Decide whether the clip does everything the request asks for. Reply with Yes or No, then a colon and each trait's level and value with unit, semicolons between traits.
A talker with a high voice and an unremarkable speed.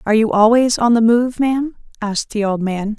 No: high, 225 Hz; fast, 220 wpm